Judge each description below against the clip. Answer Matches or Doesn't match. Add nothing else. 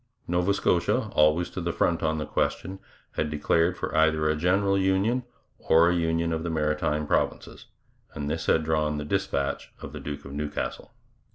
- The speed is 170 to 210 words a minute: Matches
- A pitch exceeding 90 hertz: Doesn't match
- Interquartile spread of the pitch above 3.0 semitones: Doesn't match